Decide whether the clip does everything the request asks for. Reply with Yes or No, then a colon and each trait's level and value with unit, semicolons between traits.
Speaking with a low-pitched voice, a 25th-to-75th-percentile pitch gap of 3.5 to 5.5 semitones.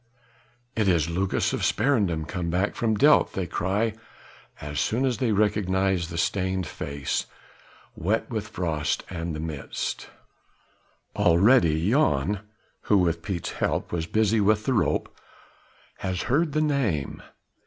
Yes: very low, 95 Hz; average, 4.6 semitones